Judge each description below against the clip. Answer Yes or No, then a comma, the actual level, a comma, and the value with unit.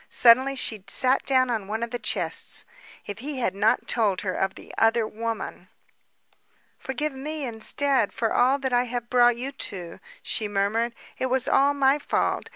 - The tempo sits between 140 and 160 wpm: No, average, 175 wpm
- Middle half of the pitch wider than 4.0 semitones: No, average, 3.3 semitones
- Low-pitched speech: No, high, 240 Hz